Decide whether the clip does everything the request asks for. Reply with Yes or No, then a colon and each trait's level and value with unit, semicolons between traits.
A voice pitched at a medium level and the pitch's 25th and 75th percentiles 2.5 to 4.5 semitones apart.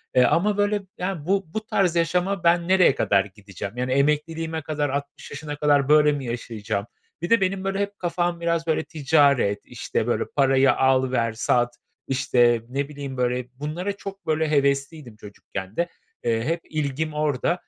No: medium, 145 Hz; average, 5.0 semitones